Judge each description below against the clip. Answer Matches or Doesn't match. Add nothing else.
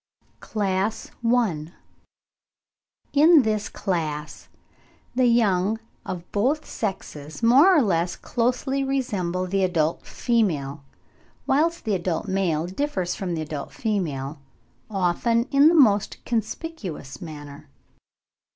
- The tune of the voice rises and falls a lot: Matches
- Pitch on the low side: Doesn't match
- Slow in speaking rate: Matches